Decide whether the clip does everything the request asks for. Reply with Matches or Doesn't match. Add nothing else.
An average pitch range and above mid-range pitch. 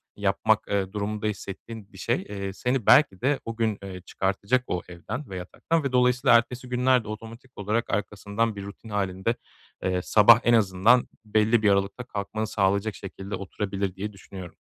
Doesn't match